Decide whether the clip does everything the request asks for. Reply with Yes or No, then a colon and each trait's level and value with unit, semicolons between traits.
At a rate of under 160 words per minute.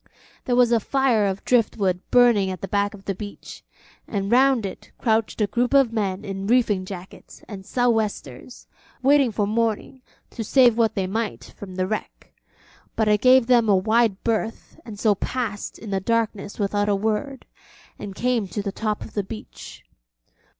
No: average, 180 wpm